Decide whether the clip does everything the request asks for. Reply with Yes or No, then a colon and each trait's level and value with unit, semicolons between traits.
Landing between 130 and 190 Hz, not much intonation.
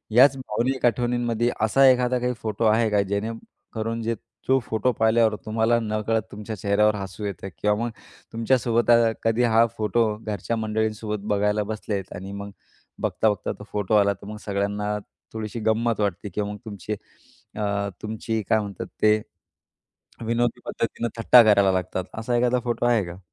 No: low, 110 Hz; narrow, 2.1 semitones